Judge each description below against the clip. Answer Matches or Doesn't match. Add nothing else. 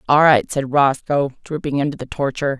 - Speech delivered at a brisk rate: Doesn't match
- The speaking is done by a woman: Matches